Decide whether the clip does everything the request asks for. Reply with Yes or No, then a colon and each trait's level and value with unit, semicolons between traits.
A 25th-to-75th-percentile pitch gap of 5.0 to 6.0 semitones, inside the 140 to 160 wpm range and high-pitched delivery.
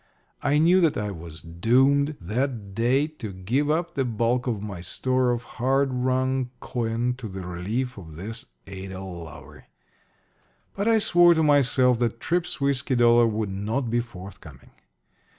No: wide, 5.4 semitones; average, 155 wpm; low, 120 Hz